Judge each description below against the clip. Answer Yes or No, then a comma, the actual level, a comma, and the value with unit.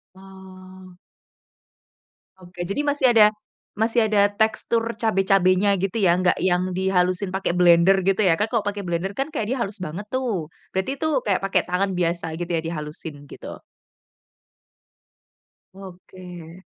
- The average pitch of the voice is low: No, high, 190 Hz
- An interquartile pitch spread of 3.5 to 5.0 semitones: No, narrow, 2.5 semitones